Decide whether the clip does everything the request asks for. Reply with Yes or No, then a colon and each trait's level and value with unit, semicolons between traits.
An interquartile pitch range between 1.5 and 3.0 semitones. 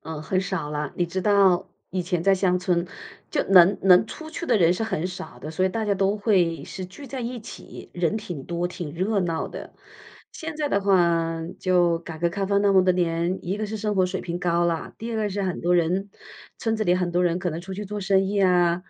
Yes: average, 2.7 semitones